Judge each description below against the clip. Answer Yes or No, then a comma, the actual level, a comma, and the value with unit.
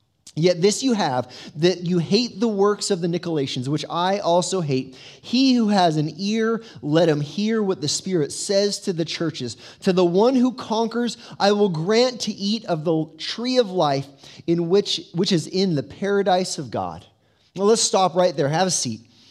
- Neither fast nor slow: Yes, average, 195 wpm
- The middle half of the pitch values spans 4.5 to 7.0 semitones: Yes, average, 5.3 semitones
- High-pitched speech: No, medium, 180 Hz